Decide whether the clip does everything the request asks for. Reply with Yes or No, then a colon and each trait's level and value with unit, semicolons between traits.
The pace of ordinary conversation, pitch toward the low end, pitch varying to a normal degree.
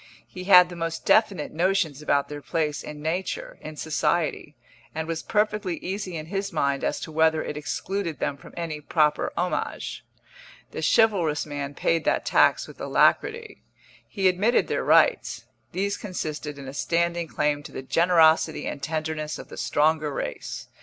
No: average, 165 wpm; medium, 160 Hz; average, 3.3 semitones